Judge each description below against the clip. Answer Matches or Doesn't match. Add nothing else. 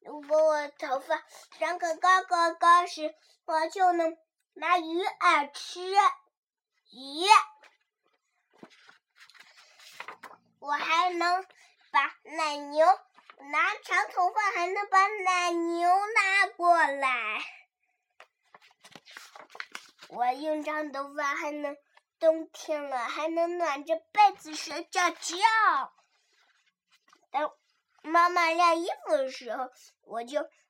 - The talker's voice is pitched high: Matches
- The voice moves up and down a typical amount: Matches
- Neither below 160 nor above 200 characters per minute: Doesn't match